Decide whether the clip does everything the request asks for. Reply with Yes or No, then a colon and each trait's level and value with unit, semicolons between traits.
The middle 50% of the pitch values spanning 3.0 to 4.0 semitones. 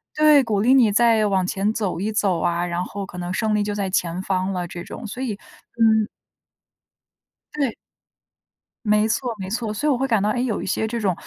Yes: average, 3.5 semitones